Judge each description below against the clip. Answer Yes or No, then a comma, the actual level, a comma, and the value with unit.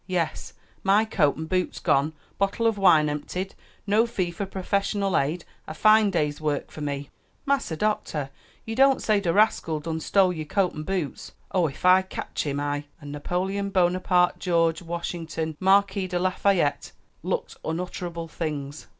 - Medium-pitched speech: Yes, medium, 180 Hz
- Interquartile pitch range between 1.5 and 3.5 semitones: No, average, 4.1 semitones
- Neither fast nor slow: Yes, average, 165 wpm